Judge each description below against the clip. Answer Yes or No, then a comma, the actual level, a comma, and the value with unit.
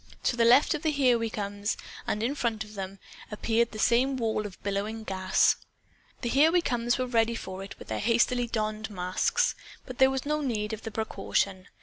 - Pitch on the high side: Yes, high, 225 Hz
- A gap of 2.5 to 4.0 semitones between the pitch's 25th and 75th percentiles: Yes, average, 3.2 semitones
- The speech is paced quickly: Yes, fast, 215 wpm